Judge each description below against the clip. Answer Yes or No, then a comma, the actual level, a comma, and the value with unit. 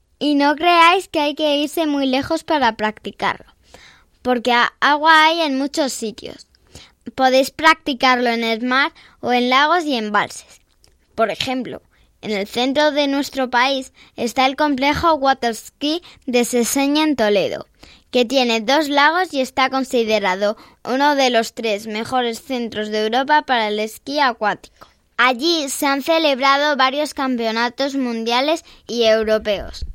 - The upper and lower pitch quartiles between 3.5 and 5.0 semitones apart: Yes, average, 4.1 semitones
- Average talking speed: Yes, average, 140 wpm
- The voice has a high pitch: Yes, very high, 260 Hz